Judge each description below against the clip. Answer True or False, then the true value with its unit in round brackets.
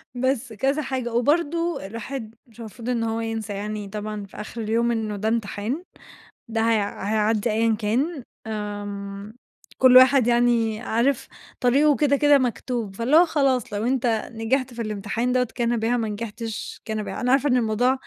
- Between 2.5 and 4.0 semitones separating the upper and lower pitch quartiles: True (3.1 semitones)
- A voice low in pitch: False (230 Hz)